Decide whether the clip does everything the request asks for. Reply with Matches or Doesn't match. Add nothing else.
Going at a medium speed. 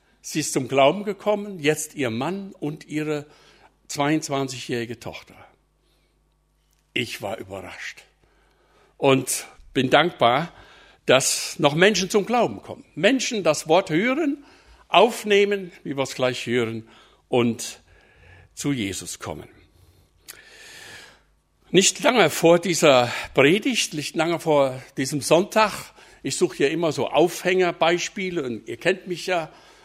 Doesn't match